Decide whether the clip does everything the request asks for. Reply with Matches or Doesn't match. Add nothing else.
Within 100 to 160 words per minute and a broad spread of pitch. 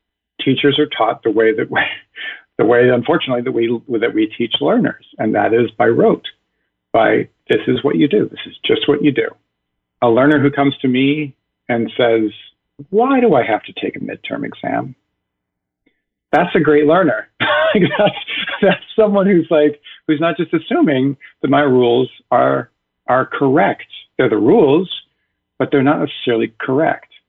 Doesn't match